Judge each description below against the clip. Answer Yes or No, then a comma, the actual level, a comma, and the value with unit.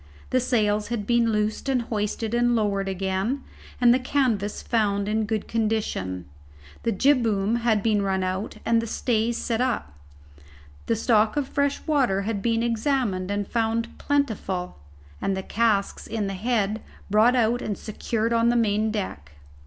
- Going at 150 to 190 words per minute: Yes, average, 160 wpm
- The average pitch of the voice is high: Yes, high, 220 Hz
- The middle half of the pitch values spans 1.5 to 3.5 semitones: Yes, average, 2.8 semitones